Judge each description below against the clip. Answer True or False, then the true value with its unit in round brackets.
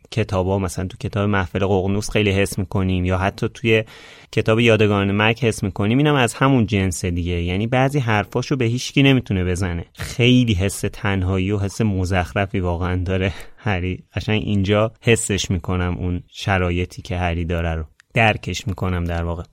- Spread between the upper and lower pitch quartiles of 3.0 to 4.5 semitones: True (3.3 semitones)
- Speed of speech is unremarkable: False (165 wpm)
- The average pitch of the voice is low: True (100 Hz)